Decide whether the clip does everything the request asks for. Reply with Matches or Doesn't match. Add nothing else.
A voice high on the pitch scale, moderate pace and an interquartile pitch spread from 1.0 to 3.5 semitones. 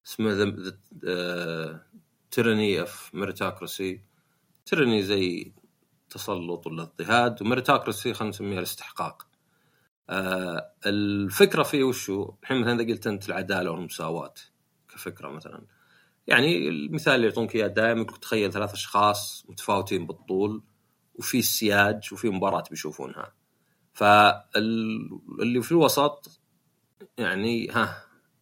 Doesn't match